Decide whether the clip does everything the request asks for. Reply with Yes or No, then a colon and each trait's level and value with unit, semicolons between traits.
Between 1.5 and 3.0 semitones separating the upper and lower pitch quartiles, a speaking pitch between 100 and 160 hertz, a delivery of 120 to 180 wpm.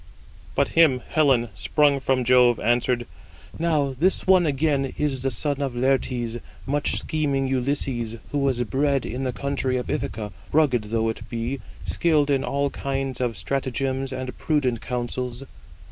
Yes: narrow, 2.5 semitones; low, 135 Hz; average, 150 wpm